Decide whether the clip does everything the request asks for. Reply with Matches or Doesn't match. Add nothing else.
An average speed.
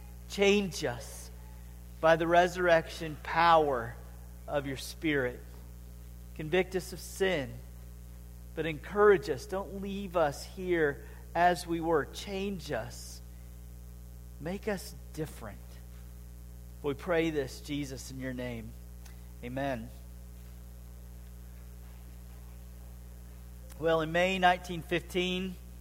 Doesn't match